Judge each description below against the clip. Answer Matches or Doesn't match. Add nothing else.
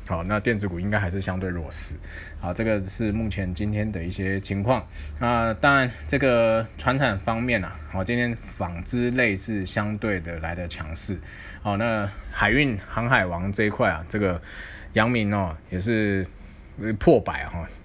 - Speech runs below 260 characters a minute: Matches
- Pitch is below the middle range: Matches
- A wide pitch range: Doesn't match